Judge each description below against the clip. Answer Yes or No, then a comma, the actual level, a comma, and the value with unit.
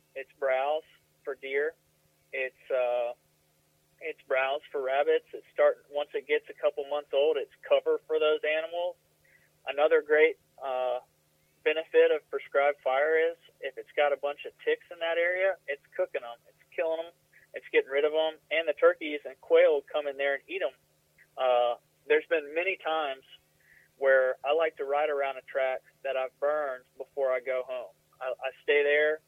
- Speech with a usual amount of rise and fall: No, wide, 6.0 semitones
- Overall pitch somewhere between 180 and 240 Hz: No, medium, 150 Hz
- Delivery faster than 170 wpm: Yes, average, 180 wpm